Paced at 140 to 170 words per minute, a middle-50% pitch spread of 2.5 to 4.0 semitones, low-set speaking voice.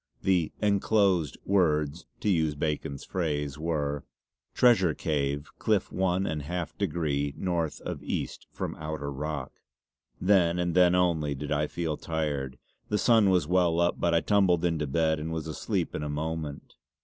Yes: average, 160 wpm; average, 3.3 semitones; very low, 80 Hz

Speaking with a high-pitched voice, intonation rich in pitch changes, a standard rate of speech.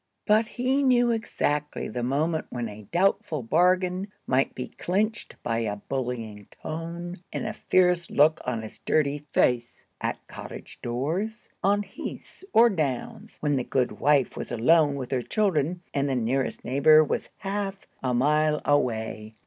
No: medium, 150 Hz; wide, 6.6 semitones; average, 155 wpm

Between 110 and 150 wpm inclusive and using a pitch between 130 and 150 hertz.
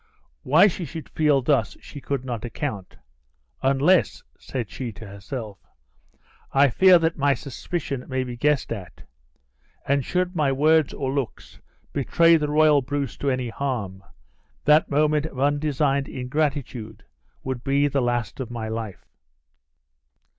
Yes: average, 140 wpm; low, 135 Hz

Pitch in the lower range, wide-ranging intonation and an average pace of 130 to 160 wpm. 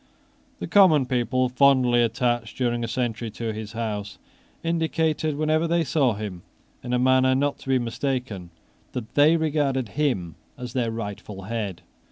No: low, 125 Hz; average, 3.9 semitones; average, 155 wpm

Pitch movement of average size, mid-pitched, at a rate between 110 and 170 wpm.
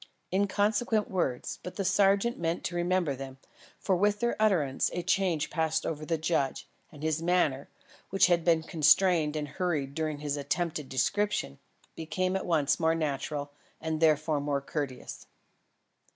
Yes: average, 4.0 semitones; medium, 160 Hz; average, 150 wpm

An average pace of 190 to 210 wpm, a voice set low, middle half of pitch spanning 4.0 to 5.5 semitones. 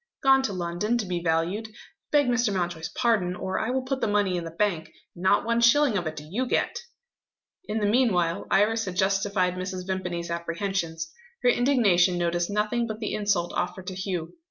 No: average, 195 wpm; high, 195 Hz; average, 4.4 semitones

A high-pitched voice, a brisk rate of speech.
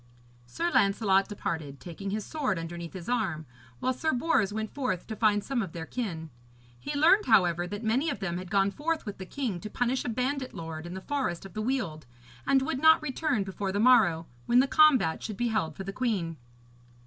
Yes: high, 210 Hz; fast, 210 wpm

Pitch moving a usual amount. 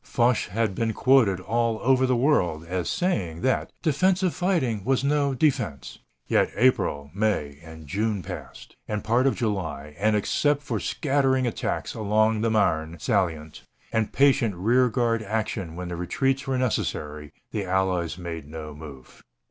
No: wide, 7.1 semitones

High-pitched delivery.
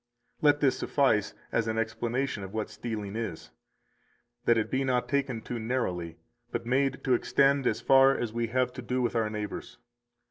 No: low, 120 Hz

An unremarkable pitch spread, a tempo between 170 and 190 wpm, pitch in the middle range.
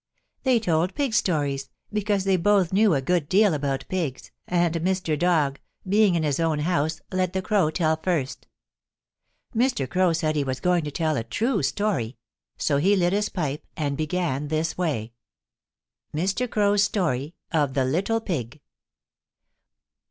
No: average, 4.6 semitones; average, 160 wpm; medium, 170 Hz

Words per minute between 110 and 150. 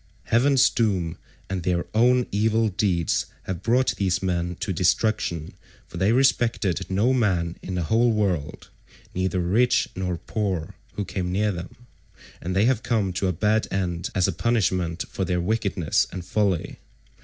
No: average, 160 wpm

